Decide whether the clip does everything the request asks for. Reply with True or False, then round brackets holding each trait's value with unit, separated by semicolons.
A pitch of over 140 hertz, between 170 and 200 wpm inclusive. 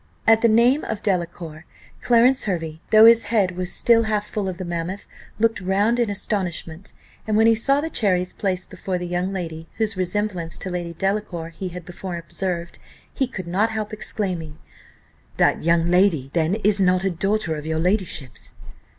True (190 Hz; 180 wpm)